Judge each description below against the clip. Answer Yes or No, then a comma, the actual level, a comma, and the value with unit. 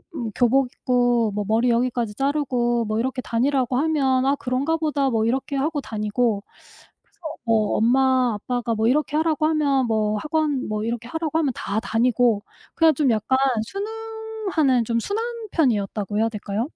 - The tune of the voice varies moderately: Yes, average, 4.3 semitones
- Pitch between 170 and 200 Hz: No, very high, 250 Hz